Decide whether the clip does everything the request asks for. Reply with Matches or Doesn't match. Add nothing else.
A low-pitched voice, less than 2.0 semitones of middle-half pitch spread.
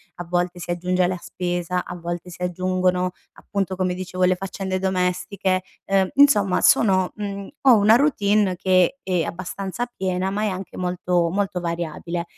Doesn't match